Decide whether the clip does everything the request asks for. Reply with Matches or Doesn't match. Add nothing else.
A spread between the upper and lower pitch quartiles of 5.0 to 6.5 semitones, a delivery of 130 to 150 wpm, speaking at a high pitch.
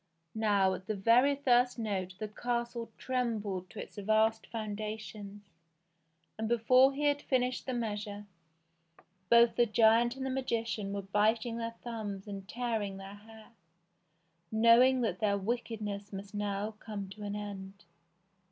Doesn't match